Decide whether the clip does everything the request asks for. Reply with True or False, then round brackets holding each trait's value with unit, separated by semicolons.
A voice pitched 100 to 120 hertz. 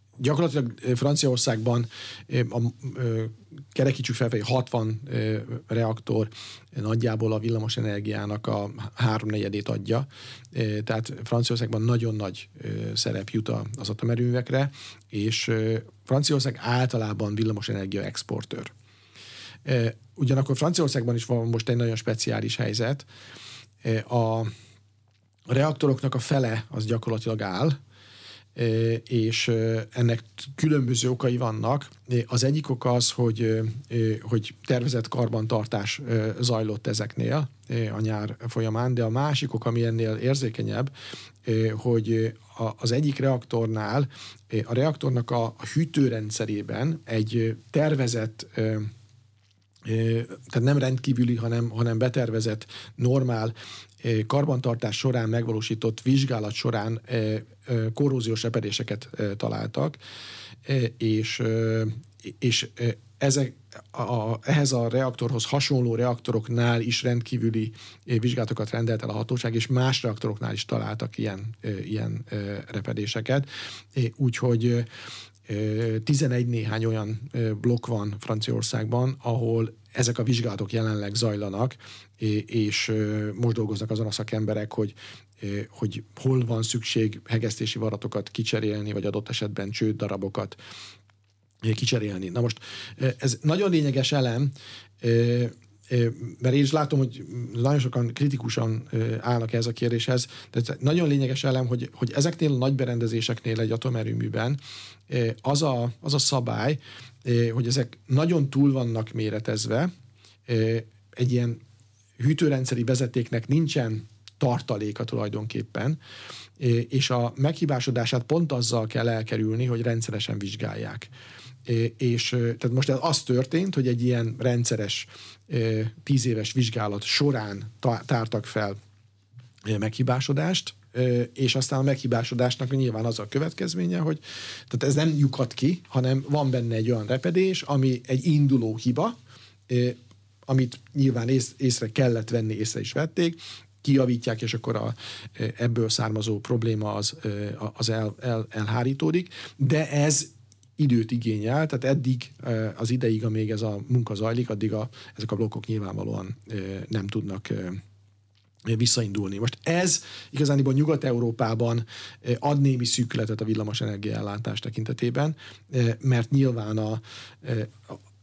True (115 Hz)